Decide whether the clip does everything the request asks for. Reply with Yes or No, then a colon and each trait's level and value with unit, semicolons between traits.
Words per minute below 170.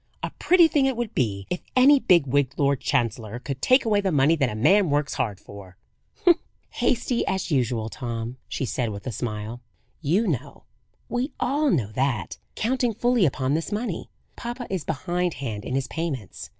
No: average, 175 wpm